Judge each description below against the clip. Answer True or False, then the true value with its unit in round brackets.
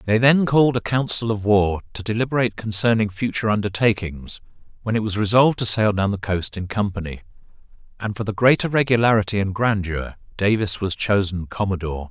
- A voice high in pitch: False (105 Hz)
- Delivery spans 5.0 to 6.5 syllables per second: True (5.9 syllables/s)